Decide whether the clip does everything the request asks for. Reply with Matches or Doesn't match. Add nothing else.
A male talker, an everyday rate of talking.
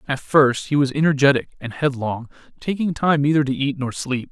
Matches